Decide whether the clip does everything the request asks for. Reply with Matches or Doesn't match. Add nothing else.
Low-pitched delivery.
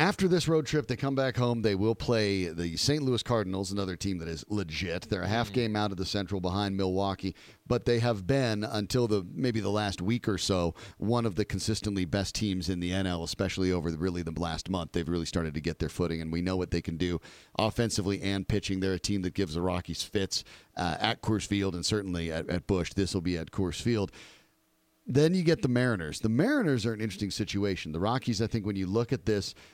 Matches